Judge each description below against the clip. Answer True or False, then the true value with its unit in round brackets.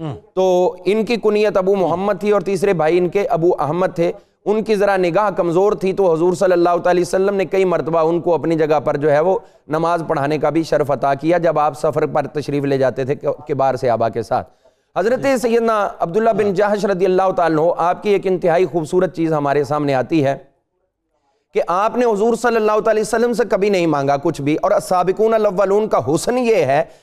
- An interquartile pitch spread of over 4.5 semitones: True (4.9 semitones)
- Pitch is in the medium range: True (180 Hz)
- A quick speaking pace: True (215 wpm)